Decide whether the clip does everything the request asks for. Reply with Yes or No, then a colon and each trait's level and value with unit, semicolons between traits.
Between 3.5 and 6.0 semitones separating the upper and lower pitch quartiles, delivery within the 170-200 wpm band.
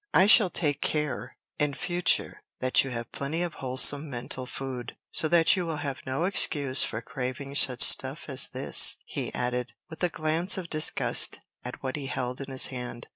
Yes: average, 4.0 semitones; average, 185 wpm